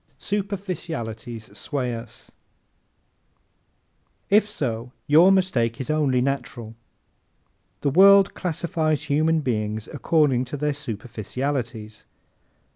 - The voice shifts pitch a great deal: Yes, wide, 5.7 semitones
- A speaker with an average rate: No, slow, 95 wpm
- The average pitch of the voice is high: No, medium, 140 Hz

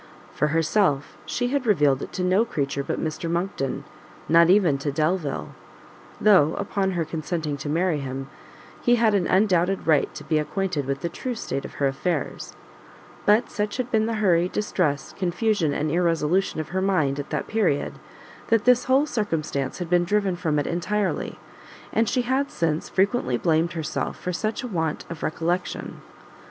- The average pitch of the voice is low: No, medium, 175 Hz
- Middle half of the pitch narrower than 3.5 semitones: No, average, 5.3 semitones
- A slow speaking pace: No, average, 170 wpm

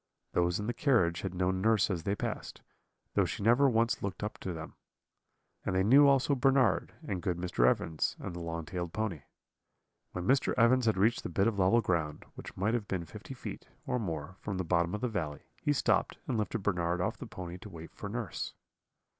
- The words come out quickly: Yes, fast, 215 wpm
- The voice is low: Yes, very low, 95 Hz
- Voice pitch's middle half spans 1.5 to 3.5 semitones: No, average, 4.7 semitones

